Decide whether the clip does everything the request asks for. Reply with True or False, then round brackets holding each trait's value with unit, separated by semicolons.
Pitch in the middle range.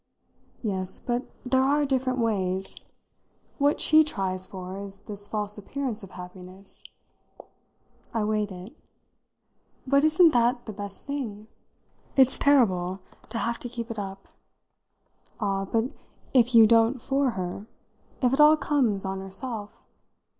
False (220 Hz)